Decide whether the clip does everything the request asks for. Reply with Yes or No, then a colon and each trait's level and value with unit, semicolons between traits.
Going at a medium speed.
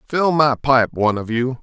No: fast, 220 wpm